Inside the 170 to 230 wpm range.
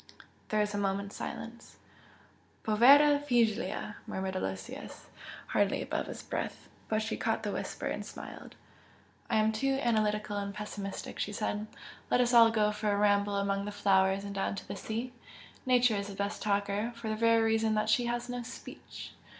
Yes: average, 175 wpm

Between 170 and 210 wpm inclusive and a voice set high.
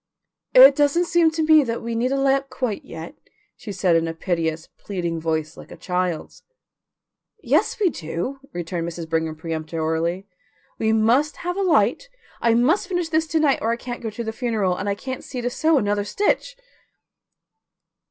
Yes: average, 180 wpm; high, 225 Hz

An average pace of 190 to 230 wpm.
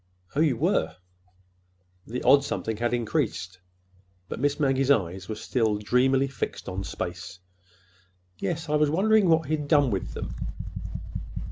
No: average, 145 wpm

